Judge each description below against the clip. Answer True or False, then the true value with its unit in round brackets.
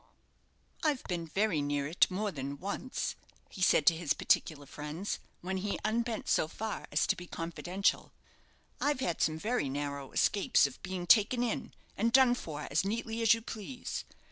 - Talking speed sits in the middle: True (170 wpm)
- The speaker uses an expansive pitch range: True (6.4 semitones)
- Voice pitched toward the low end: False (190 Hz)